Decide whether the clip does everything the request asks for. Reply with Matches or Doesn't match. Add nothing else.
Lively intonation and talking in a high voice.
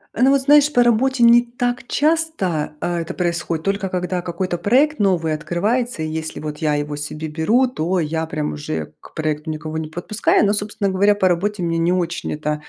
Doesn't match